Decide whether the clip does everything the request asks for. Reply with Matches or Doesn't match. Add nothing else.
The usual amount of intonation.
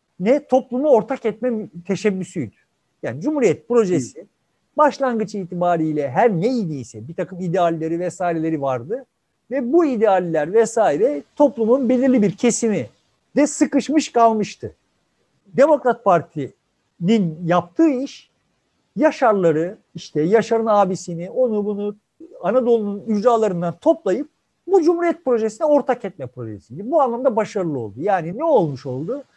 Doesn't match